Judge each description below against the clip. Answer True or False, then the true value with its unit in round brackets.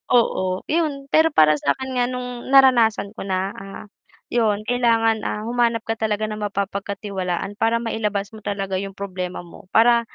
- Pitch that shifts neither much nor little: True (3.4 semitones)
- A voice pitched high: True (215 Hz)